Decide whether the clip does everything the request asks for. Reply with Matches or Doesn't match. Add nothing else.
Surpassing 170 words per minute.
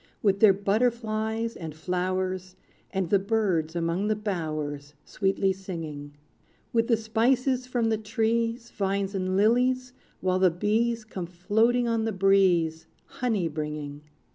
Doesn't match